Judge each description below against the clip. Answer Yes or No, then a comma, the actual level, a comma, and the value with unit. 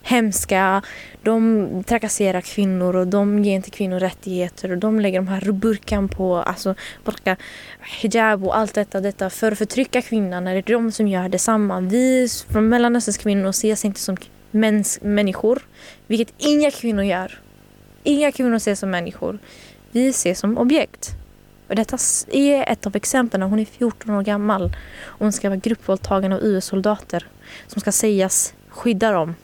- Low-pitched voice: No, high, 210 Hz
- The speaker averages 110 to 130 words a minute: No, average, 160 wpm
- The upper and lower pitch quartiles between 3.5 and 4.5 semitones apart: No, average, 2.8 semitones